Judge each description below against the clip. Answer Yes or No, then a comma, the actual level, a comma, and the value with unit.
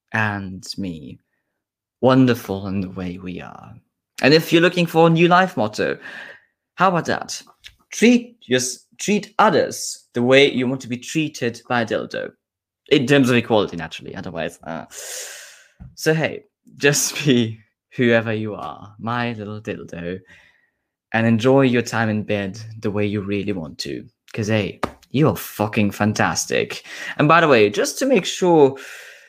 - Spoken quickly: Yes, fast, 155 wpm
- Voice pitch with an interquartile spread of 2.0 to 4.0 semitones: No, average, 4.7 semitones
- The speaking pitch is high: No, low, 115 Hz